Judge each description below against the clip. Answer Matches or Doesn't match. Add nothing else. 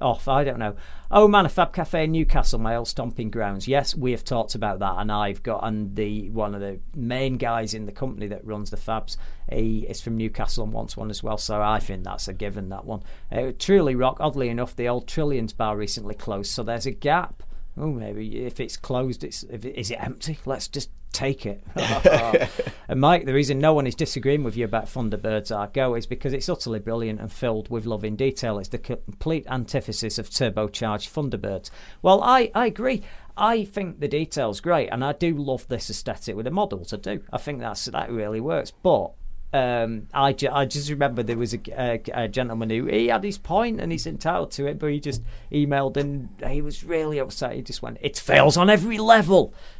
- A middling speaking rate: Doesn't match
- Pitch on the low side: Matches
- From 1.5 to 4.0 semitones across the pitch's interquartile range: Doesn't match